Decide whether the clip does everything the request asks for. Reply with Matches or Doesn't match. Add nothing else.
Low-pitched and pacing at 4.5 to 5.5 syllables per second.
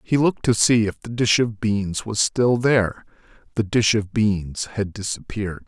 Matches